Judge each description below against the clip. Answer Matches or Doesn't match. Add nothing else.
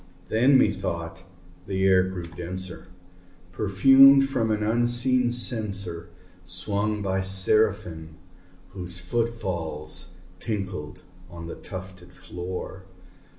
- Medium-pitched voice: Doesn't match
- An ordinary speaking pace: Doesn't match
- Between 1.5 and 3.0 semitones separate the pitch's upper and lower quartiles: Doesn't match